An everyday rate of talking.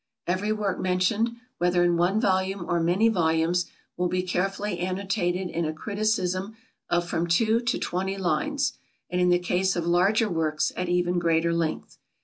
Yes: average, 165 wpm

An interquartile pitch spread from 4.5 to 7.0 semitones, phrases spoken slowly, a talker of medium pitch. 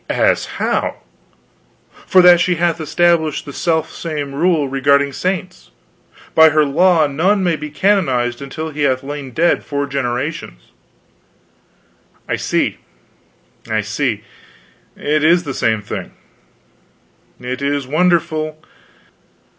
No: average, 3.8 semitones; slow, 120 wpm; medium, 150 Hz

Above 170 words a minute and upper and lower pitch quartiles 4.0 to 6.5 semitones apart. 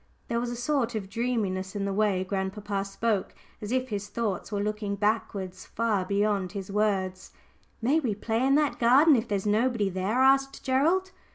No: average, 185 wpm; average, 3.6 semitones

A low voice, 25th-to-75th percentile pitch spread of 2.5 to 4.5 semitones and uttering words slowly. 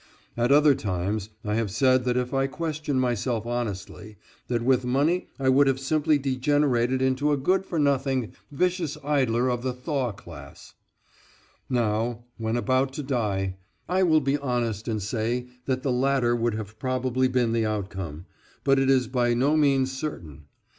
No: low, 130 Hz; average, 3.2 semitones; average, 165 wpm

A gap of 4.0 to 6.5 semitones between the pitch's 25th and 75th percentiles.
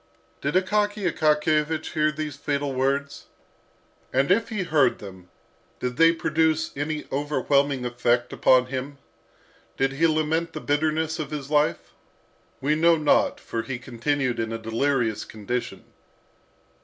No: average, 3.5 semitones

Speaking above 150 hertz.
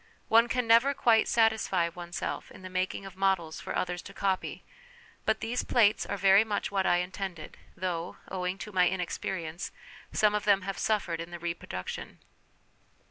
Yes: high, 190 Hz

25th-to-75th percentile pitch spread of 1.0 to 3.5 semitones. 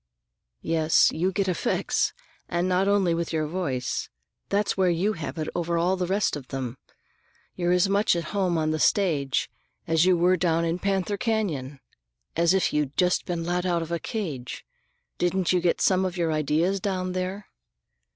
Yes: average, 2.7 semitones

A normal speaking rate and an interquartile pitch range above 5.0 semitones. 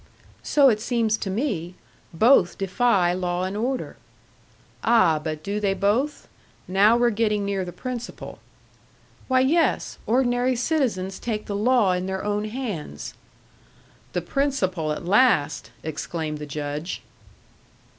No: slow, 130 wpm; wide, 5.4 semitones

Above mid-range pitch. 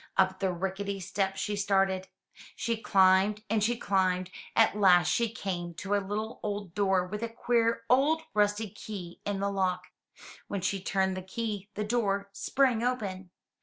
Yes: high, 200 Hz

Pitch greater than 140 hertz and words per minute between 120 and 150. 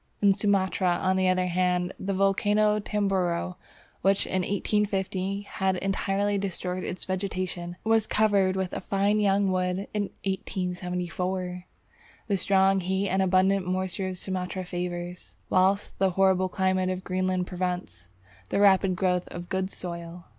Yes: medium, 185 Hz; average, 145 wpm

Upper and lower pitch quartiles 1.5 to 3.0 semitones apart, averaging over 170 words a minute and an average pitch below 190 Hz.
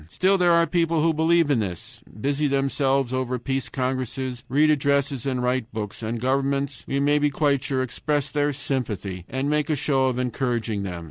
Yes: average, 2.7 semitones; average, 190 wpm; low, 135 Hz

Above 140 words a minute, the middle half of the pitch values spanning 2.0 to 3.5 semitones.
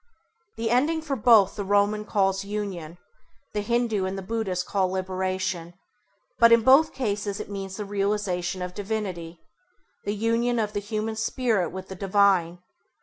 Yes: average, 155 wpm; average, 2.8 semitones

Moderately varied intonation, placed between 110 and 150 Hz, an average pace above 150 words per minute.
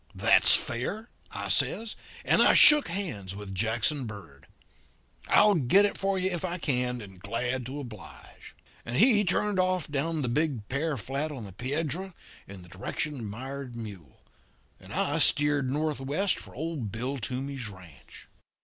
No: wide, 6.7 semitones; low, 135 Hz; average, 160 wpm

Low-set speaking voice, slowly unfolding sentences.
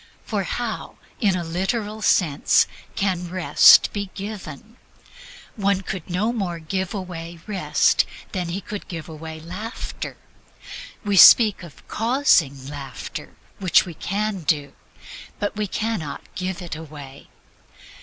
No: medium, 185 Hz; slow, 130 wpm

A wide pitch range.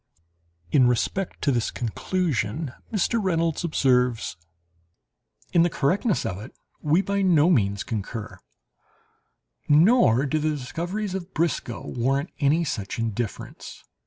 Yes: wide, 6.3 semitones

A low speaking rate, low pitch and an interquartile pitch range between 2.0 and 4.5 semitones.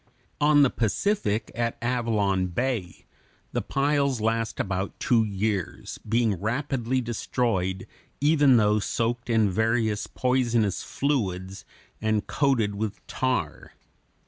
Yes: slow, 110 wpm; low, 115 Hz; average, 3.6 semitones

